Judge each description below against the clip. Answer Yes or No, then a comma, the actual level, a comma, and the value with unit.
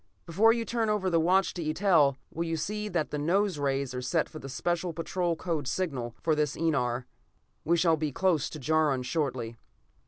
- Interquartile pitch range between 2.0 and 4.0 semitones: No, average, 4.4 semitones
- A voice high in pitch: No, medium, 160 Hz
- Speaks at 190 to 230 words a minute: Yes, average, 195 wpm